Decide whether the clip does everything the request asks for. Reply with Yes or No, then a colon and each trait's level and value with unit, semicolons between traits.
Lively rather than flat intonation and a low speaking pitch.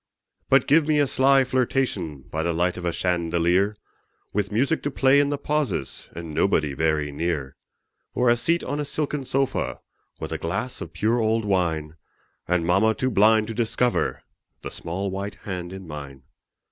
Yes: wide, 7.5 semitones; low, 100 Hz